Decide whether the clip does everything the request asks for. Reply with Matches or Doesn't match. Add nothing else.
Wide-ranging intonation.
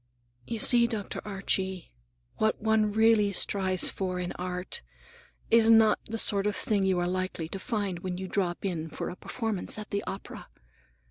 Doesn't match